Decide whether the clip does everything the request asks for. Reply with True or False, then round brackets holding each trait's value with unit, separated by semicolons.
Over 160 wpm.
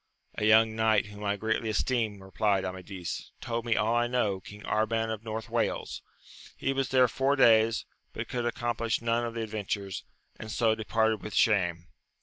True (175 wpm)